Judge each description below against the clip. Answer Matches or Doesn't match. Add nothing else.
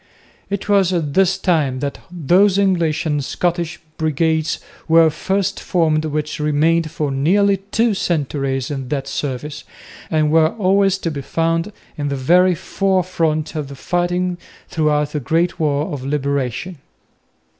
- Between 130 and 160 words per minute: Matches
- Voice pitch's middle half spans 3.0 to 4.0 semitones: Matches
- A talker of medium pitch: Matches